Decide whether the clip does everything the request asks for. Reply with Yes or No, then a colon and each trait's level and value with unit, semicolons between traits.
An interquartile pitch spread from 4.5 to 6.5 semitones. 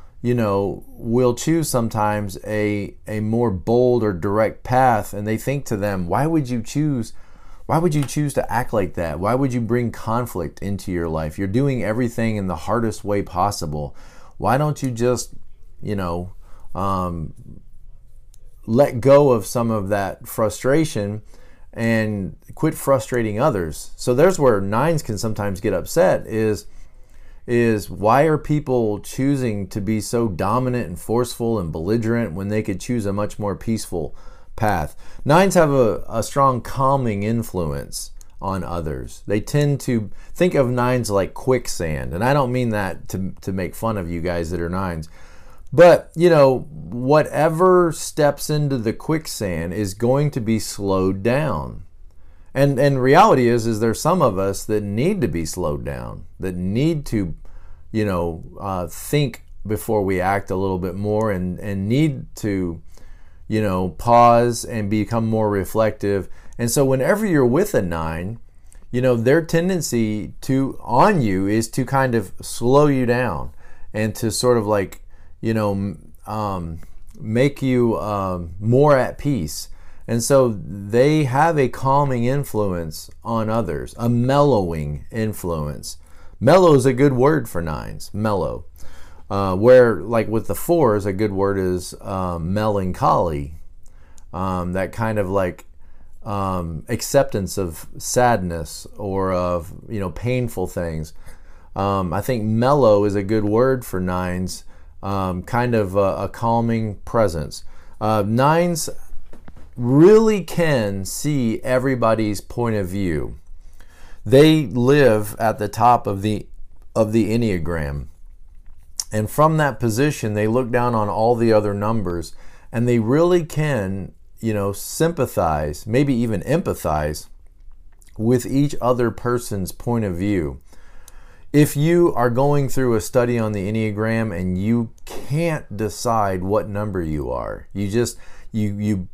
Yes: wide, 5.5 semitones